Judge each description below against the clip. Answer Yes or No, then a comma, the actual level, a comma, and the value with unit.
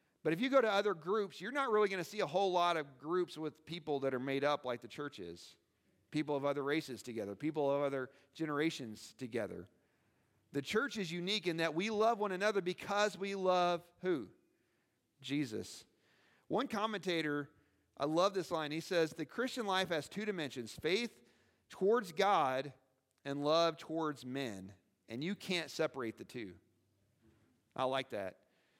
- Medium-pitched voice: Yes, medium, 155 Hz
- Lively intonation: Yes, wide, 6.1 semitones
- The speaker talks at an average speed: Yes, average, 175 wpm